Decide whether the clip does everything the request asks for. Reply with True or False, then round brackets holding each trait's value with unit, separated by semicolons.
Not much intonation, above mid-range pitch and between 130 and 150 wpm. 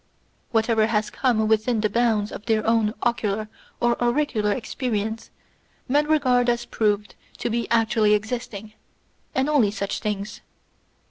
True (2.2 semitones; 225 Hz; 135 wpm)